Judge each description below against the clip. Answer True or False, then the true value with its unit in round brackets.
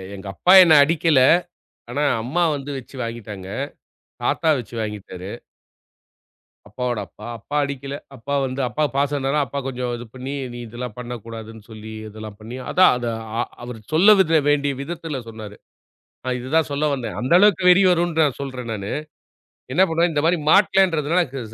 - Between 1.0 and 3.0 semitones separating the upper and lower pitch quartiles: False (5.6 semitones)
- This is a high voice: False (135 Hz)